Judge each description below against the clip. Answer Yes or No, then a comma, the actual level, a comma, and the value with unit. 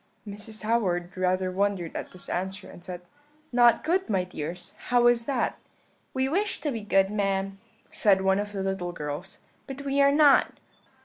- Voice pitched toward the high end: Yes, high, 200 Hz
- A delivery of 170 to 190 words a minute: Yes, average, 175 wpm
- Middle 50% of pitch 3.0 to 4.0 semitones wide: No, average, 4.7 semitones